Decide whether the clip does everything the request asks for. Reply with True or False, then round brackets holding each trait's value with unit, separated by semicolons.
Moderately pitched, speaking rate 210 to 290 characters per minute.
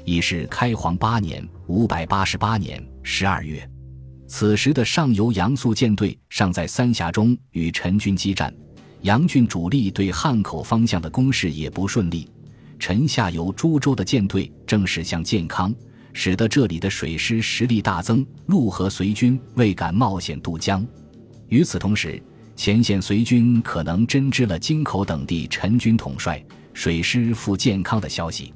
False (100 Hz; 235 characters per minute)